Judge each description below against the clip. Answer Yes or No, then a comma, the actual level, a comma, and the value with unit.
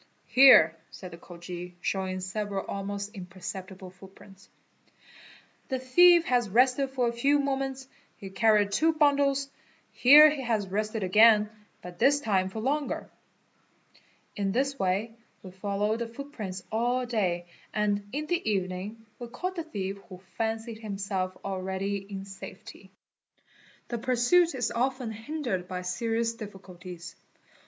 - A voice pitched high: Yes, high, 215 Hz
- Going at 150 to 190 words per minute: No, slow, 135 wpm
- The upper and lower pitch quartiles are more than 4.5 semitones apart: Yes, average, 5.0 semitones